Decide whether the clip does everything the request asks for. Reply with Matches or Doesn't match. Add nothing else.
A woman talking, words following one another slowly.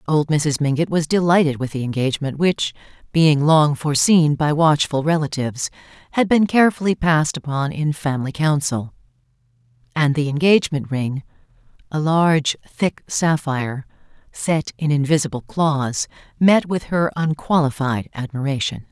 Matches